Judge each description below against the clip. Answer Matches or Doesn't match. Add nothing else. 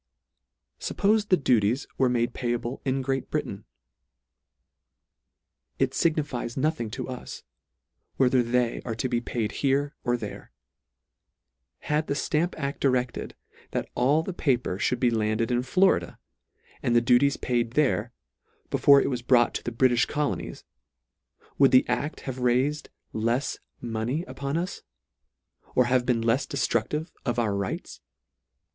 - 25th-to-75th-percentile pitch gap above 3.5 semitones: Doesn't match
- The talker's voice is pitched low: Matches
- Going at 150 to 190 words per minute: Doesn't match